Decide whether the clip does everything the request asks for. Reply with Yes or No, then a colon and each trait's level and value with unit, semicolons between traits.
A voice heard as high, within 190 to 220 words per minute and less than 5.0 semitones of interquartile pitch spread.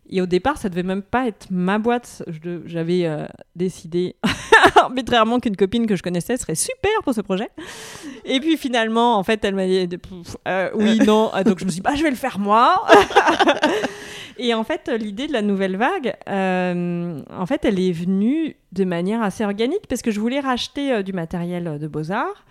No: high, 215 Hz; average, 205 wpm; wide, 5.5 semitones